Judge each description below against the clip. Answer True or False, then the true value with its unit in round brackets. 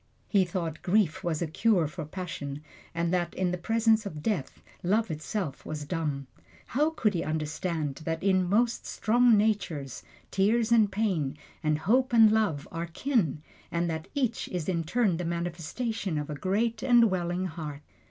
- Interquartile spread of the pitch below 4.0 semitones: False (5.5 semitones)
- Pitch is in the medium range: True (180 Hz)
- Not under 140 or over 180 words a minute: True (170 wpm)